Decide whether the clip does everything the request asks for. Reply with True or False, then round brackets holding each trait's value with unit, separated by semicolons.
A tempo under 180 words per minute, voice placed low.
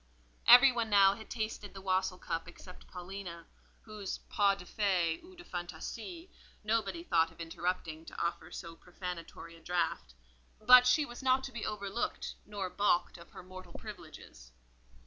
False (160 wpm; 190 Hz)